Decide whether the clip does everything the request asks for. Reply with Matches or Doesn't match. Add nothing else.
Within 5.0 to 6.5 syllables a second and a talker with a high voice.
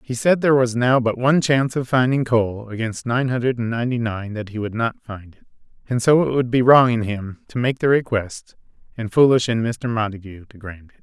Doesn't match